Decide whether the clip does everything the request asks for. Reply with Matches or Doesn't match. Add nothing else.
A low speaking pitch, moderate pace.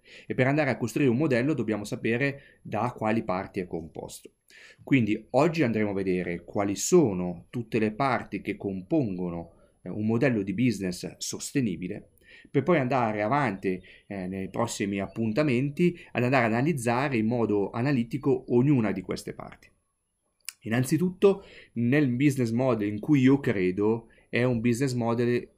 Matches